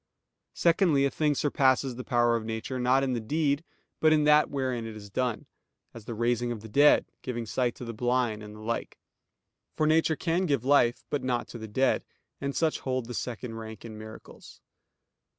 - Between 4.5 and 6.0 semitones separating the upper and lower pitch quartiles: No, average, 3.6 semitones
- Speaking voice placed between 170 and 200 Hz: No, low, 125 Hz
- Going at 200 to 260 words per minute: Yes, fast, 205 wpm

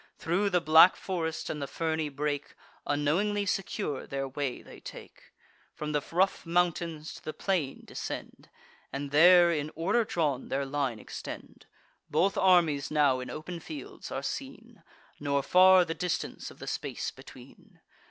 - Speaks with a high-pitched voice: No, medium, 160 Hz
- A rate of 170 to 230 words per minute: No, average, 150 wpm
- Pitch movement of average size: Yes, average, 3.6 semitones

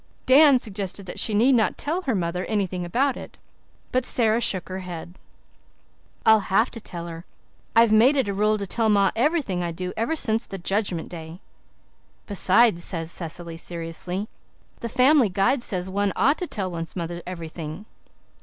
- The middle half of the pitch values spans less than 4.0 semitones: No, average, 4.8 semitones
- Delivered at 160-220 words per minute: Yes, average, 175 wpm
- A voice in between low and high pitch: No, high, 200 Hz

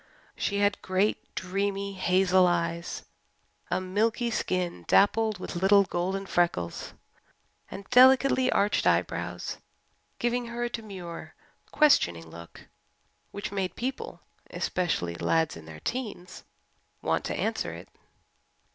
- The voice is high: Yes, high, 195 Hz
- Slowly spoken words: Yes, slow, 115 wpm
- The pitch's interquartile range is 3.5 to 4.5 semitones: Yes, average, 3.8 semitones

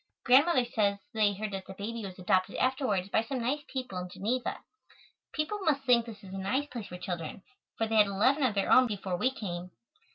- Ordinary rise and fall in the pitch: Yes, average, 4.9 semitones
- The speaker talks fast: Yes, fast, 215 wpm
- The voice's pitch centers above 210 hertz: Yes, high, 220 Hz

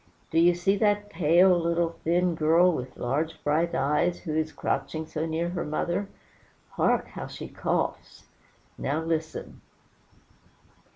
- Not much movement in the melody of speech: Yes, narrow, 1.9 semitones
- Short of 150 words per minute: Yes, slow, 135 wpm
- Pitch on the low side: No, medium, 165 Hz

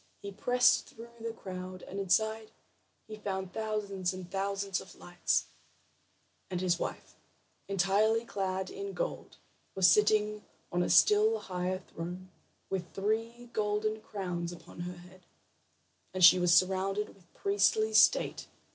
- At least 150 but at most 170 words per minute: No, slow, 135 wpm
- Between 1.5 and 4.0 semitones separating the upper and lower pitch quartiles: Yes, average, 3.0 semitones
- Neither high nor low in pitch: No, high, 195 Hz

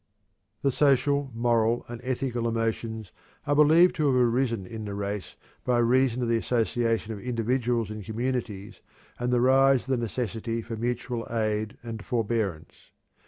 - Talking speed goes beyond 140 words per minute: Yes, average, 155 wpm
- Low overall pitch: Yes, low, 115 Hz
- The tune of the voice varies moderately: No, narrow, 2.2 semitones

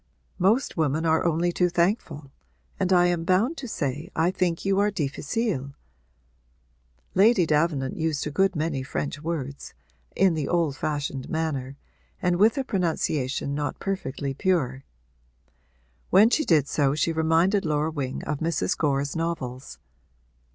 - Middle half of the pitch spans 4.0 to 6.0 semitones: Yes, average, 4.3 semitones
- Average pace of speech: Yes, average, 145 wpm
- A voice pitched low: No, medium, 160 Hz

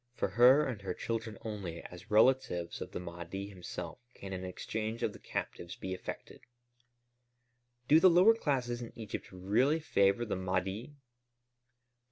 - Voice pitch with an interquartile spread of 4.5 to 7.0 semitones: Yes, average, 4.9 semitones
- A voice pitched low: Yes, low, 105 Hz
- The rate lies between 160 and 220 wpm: No, average, 150 wpm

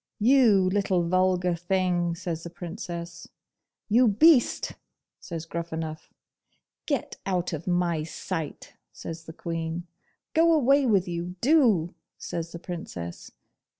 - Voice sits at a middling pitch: Yes, medium, 175 Hz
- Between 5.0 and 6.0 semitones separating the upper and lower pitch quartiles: No, average, 3.3 semitones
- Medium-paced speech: No, slow, 115 wpm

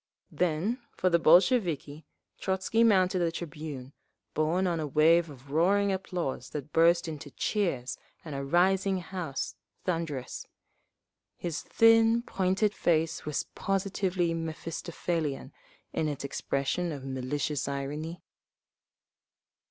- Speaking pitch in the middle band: Yes, medium, 165 Hz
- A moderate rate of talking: No, slow, 115 wpm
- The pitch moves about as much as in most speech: Yes, average, 4.0 semitones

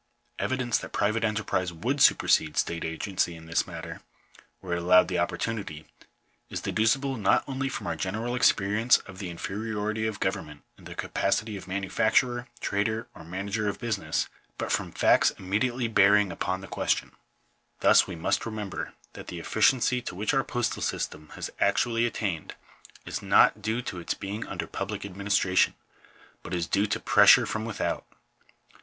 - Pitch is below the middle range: Yes, low, 105 Hz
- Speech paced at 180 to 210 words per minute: No, average, 165 wpm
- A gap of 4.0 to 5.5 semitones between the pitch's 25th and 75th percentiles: No, average, 3.5 semitones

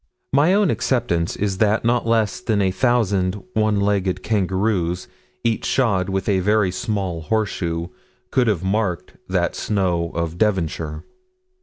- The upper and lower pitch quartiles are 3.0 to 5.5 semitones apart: Yes, average, 3.4 semitones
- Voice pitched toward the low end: Yes, low, 100 Hz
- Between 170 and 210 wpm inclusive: No, average, 140 wpm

